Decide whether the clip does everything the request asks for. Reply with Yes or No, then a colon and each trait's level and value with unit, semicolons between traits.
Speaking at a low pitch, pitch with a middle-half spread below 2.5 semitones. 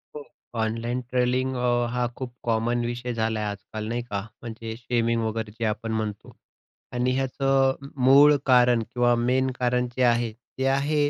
Yes: low, 120 Hz; narrow, 2.0 semitones